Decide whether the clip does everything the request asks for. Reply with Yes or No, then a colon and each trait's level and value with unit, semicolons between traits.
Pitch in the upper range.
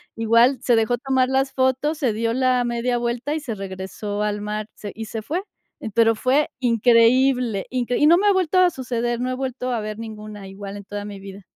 Yes: high, 235 Hz